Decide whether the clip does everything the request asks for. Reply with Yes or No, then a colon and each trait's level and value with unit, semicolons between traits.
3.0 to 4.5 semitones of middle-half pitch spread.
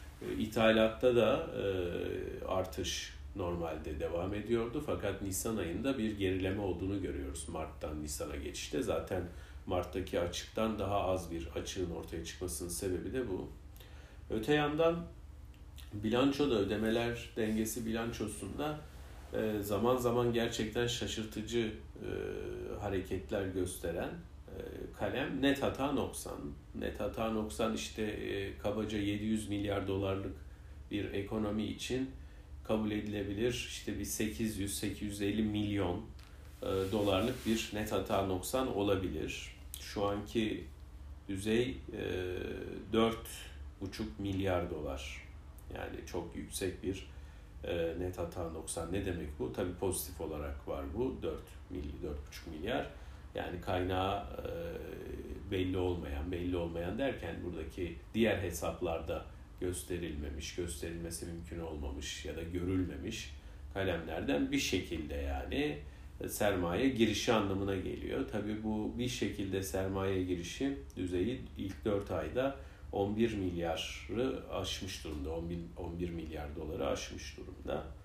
No: average, 5.0 semitones